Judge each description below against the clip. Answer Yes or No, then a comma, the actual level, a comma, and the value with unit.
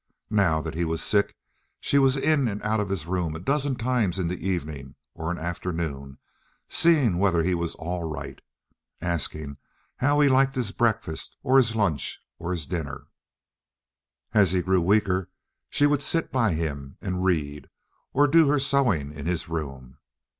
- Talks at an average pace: Yes, average, 170 wpm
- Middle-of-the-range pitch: No, very low, 90 Hz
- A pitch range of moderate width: No, wide, 7.3 semitones